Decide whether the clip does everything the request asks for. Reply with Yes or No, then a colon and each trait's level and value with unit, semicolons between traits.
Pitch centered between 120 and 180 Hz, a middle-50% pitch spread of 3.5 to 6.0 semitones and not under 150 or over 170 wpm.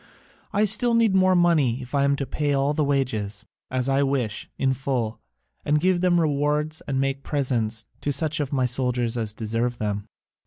No: low, 135 Hz; average, 3.8 semitones; average, 185 wpm